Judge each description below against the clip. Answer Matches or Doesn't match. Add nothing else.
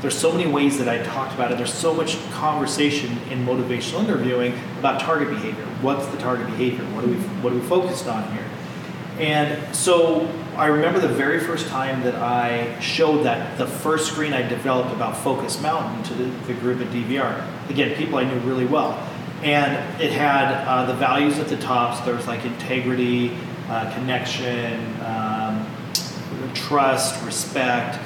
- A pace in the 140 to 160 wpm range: Doesn't match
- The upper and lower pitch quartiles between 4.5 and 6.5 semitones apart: Doesn't match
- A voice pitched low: Matches